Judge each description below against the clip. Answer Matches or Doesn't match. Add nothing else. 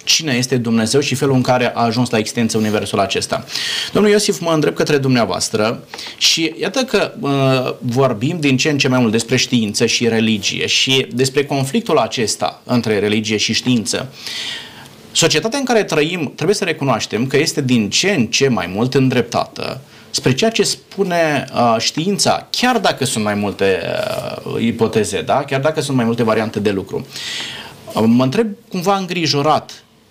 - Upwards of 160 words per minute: Matches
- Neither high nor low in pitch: Doesn't match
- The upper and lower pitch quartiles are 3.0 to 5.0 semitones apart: Doesn't match